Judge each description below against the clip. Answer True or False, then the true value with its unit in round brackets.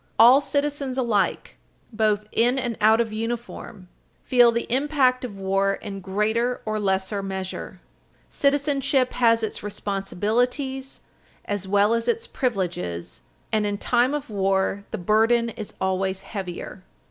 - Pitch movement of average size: True (4.1 semitones)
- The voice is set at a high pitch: True (220 Hz)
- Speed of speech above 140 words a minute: False (135 wpm)